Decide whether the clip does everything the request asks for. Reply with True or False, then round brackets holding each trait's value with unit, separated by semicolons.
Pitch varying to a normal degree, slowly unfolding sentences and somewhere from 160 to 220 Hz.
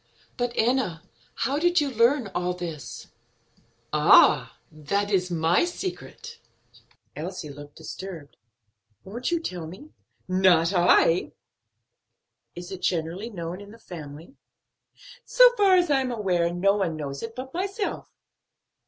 False (7.6 semitones; 130 wpm; 190 Hz)